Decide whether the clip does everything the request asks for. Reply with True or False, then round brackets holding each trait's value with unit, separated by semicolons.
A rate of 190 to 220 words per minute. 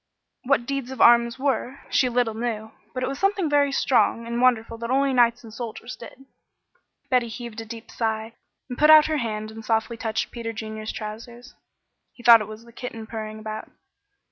True (195 wpm)